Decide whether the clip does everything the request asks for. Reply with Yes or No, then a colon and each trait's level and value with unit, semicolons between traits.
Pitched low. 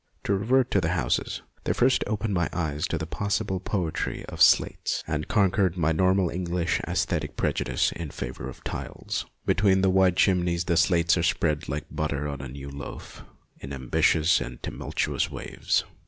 Yes: very low, 85 Hz